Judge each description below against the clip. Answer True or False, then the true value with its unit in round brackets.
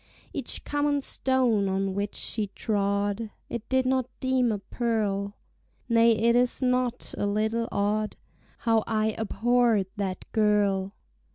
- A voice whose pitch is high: True (220 Hz)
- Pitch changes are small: False (3.1 semitones)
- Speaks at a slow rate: True (130 wpm)